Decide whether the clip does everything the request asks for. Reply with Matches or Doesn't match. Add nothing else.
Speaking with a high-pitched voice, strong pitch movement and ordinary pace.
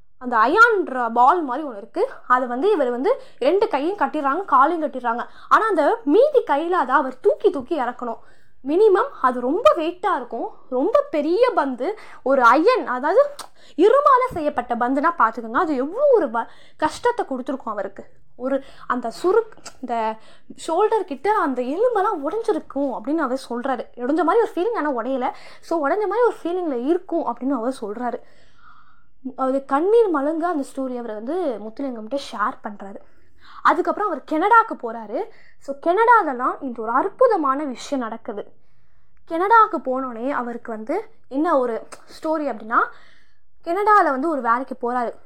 Doesn't match